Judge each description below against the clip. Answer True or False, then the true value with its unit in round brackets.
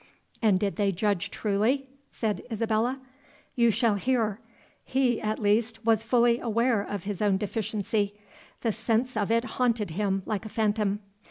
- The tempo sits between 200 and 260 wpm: False (155 wpm)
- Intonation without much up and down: True (2.3 semitones)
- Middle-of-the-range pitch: False (220 Hz)